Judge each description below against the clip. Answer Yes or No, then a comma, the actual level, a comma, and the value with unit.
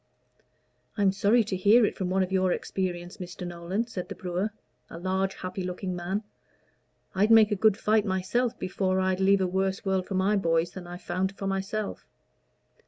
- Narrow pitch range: Yes, narrow, 1.8 semitones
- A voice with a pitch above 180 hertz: Yes, high, 190 Hz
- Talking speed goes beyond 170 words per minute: Yes, average, 190 wpm